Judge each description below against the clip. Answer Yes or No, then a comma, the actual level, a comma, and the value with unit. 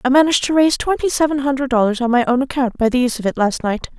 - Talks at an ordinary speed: No, fast, 285 wpm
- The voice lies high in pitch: Yes, very high, 260 Hz